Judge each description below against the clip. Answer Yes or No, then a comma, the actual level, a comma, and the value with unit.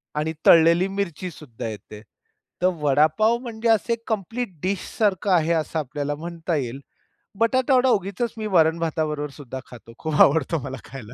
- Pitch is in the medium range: Yes, medium, 165 Hz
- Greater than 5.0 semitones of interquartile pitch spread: Yes, wide, 5.5 semitones